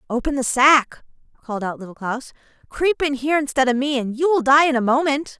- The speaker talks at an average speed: No, fast, 225 wpm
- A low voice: No, very high, 270 Hz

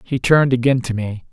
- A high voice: No, low, 125 Hz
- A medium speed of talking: No, fast, 225 wpm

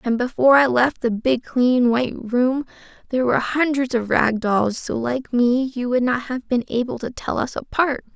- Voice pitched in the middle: No, high, 245 Hz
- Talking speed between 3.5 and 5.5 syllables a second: Yes, 4.8 syllables/s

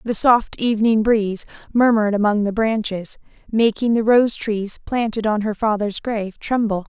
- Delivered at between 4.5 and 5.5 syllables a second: Yes, 4.9 syllables/s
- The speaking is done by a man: No, female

